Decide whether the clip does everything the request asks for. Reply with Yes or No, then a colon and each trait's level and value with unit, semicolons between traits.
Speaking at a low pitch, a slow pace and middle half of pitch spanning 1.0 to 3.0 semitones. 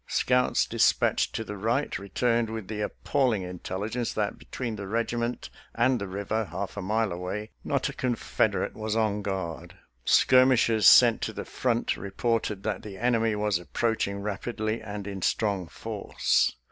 No: low, 110 Hz; average, 160 wpm; narrow, 2.6 semitones